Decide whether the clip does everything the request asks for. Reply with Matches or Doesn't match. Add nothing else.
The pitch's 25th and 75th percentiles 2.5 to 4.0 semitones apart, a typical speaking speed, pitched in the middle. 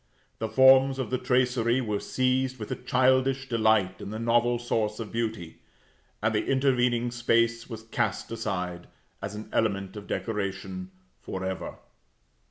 Doesn't match